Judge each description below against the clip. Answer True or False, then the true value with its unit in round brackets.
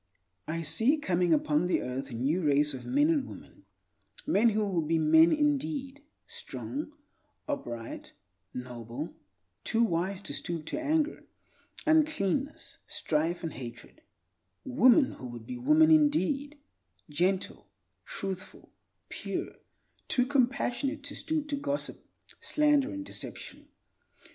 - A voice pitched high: True (230 Hz)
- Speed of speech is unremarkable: False (120 wpm)